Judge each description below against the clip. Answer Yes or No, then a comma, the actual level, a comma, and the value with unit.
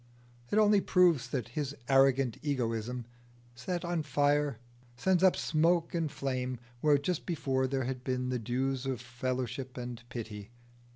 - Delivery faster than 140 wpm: Yes, average, 150 wpm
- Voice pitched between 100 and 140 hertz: Yes, low, 135 Hz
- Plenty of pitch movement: No, average, 3.5 semitones